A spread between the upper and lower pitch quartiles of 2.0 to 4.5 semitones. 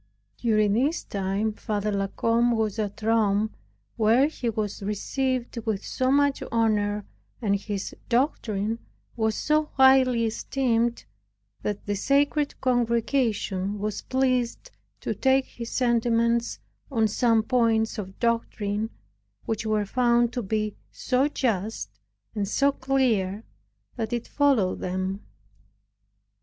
Yes: average, 3.2 semitones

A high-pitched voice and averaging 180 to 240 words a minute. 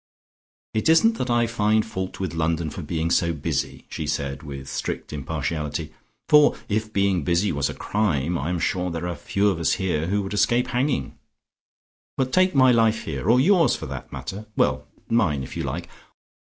No: very low, 95 Hz; average, 190 wpm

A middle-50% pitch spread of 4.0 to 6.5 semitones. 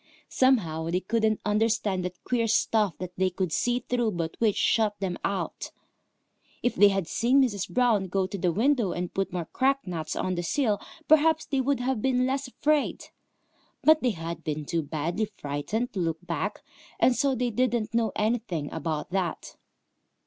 Yes: wide, 5.6 semitones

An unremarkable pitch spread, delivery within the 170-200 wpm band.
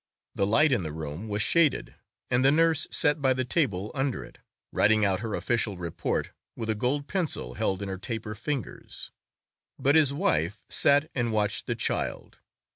No: wide, 5.9 semitones; average, 180 wpm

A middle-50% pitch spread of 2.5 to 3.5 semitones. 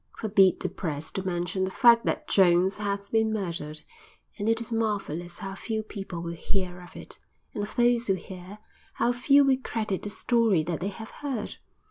No: average, 4.1 semitones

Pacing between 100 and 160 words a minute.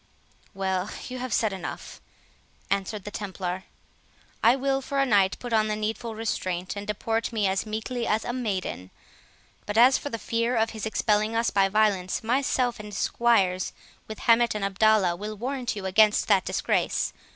No: average, 175 wpm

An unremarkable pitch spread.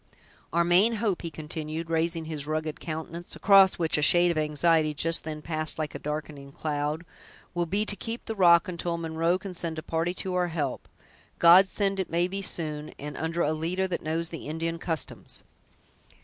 No: narrow, 2.2 semitones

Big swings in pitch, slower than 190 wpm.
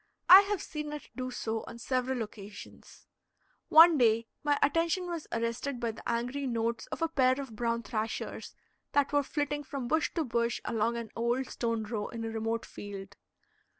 No: average, 4.2 semitones; average, 180 wpm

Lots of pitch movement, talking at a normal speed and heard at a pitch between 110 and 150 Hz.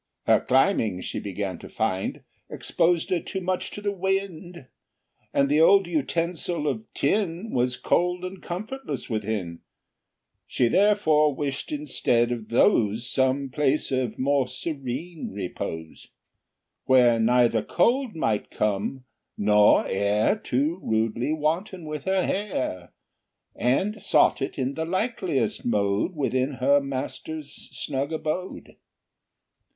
No: wide, 7.0 semitones; slow, 125 wpm; medium, 140 Hz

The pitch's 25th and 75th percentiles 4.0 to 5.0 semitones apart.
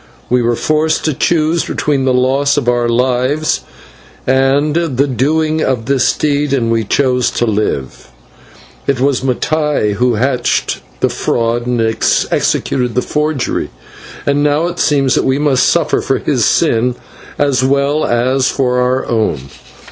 No: average, 2.9 semitones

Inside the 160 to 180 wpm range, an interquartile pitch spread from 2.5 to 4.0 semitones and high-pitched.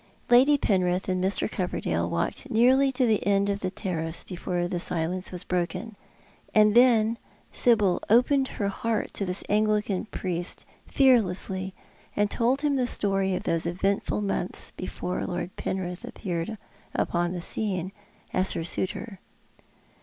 No: average, 145 wpm; average, 3.7 semitones; high, 195 Hz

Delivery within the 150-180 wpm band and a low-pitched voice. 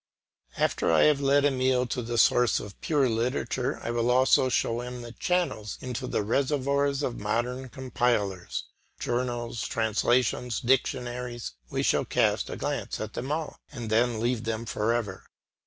Yes: average, 155 wpm; low, 120 Hz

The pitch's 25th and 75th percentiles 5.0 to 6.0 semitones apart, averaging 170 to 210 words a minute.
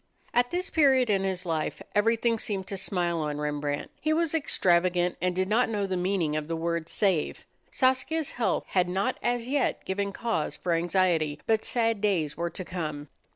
Yes: wide, 5.4 semitones; average, 185 wpm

